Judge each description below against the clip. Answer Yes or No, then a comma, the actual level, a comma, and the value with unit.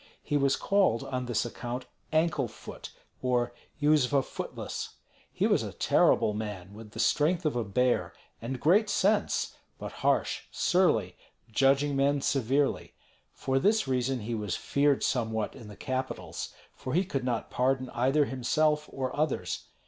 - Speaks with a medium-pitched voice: No, low, 130 Hz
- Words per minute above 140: Yes, average, 150 wpm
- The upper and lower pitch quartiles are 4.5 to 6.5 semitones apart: No, average, 3.6 semitones